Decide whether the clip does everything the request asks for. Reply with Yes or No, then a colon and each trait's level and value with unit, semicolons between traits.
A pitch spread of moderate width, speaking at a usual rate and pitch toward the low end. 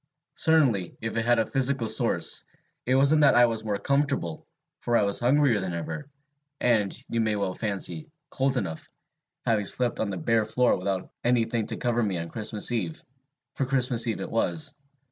Yes: average, 4.0 semitones; average, 185 wpm; low, 115 Hz